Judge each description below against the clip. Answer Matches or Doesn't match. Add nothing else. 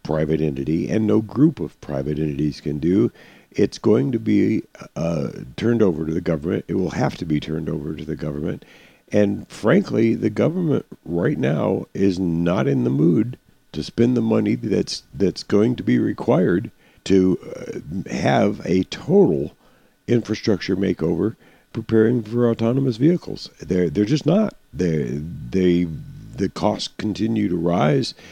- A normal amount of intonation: Doesn't match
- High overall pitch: Doesn't match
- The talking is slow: Doesn't match